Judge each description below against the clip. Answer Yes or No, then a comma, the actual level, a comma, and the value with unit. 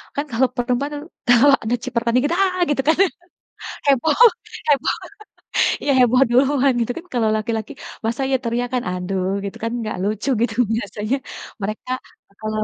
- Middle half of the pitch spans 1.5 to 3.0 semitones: No, average, 3.9 semitones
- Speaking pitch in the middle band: No, high, 245 Hz